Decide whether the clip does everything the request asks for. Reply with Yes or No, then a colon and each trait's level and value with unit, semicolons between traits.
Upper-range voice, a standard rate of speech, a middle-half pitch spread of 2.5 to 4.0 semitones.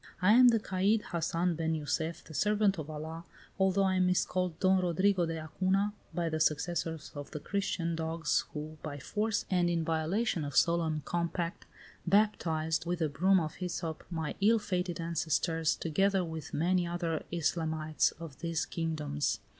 No: medium, 170 Hz; average, 160 wpm; average, 2.8 semitones